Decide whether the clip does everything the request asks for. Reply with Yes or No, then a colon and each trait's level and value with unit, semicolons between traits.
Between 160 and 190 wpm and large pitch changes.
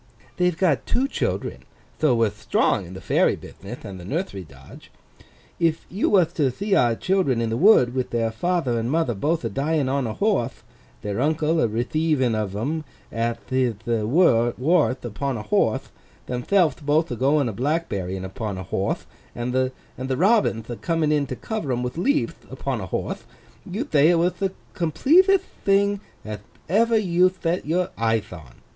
Yes: average, 170 wpm; wide, 7.0 semitones